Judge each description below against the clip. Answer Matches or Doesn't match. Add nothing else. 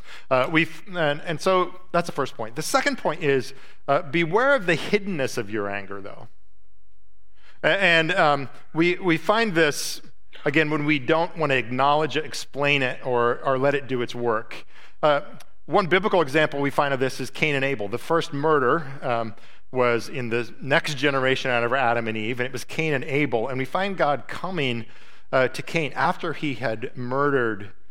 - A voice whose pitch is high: Doesn't match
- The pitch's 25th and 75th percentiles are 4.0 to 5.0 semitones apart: Matches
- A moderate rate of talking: Matches